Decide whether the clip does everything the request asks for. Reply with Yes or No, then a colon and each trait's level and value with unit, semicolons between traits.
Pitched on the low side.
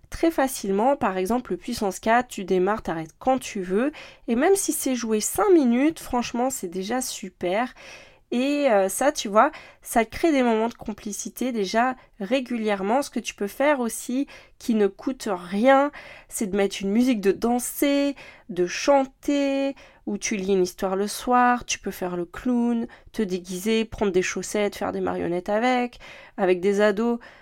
No: high, 230 Hz